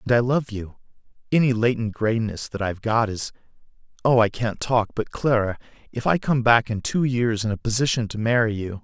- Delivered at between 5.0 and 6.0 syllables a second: Yes, 5.4 syllables/s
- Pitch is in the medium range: No, low, 115 Hz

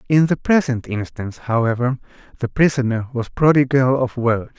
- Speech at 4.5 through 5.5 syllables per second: Yes, 5.1 syllables/s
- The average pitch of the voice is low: Yes, low, 125 Hz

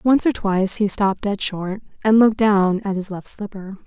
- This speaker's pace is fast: Yes, fast, 215 wpm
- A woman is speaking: Yes, female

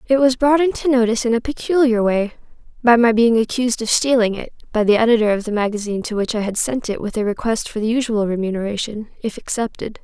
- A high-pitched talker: Yes, high, 230 Hz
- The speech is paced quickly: Yes, fast, 215 wpm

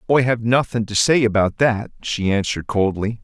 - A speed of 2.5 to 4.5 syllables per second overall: No, 5.1 syllables/s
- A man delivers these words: Yes, male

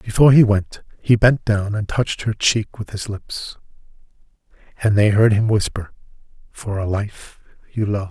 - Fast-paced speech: No, average, 170 wpm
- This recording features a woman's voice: No, male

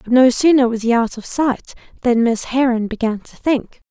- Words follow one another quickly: Yes, fast, 215 wpm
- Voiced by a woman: Yes, female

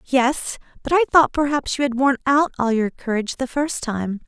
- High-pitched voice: Yes, very high, 265 Hz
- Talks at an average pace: No, fast, 210 wpm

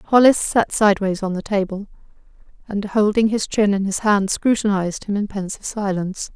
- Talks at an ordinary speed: Yes, average, 170 wpm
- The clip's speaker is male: No, female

